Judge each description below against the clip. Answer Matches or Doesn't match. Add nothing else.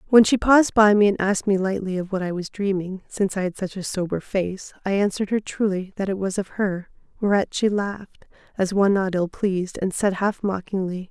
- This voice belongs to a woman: Matches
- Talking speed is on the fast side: Matches